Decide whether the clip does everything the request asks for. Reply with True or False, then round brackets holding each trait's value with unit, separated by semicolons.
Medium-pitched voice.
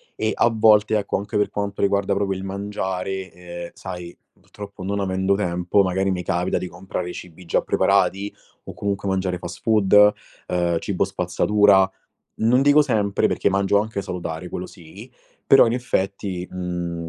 False (95 Hz)